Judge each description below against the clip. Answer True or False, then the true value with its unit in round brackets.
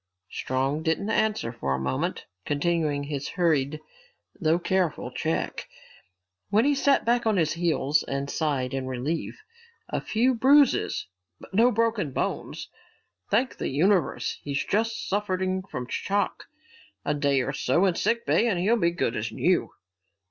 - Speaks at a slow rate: False (150 wpm)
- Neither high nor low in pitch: True (170 Hz)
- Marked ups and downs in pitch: True (6.9 semitones)